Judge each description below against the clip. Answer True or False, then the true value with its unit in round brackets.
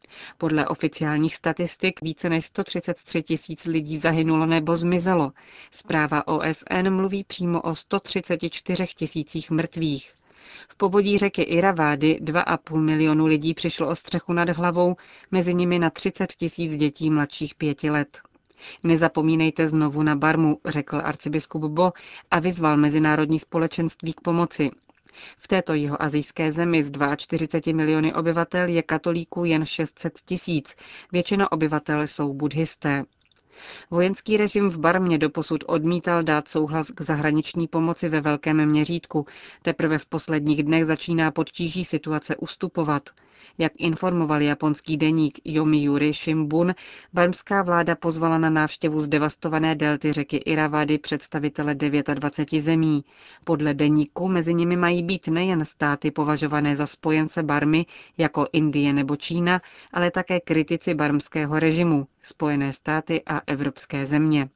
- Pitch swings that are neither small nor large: False (1.9 semitones)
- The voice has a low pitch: False (160 Hz)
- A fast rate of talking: False (125 wpm)